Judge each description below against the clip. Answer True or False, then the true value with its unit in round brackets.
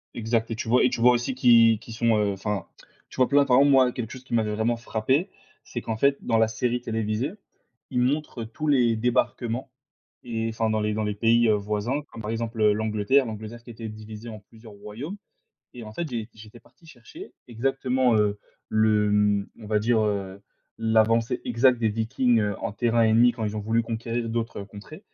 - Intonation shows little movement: True (2.2 semitones)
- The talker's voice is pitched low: True (115 Hz)